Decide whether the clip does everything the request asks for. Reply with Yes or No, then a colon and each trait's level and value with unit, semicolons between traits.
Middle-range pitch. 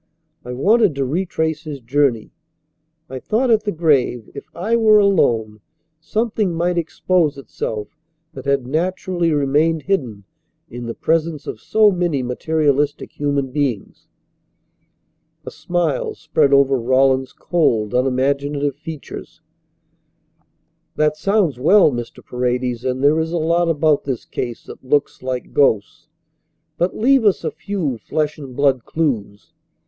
Yes: medium, 145 Hz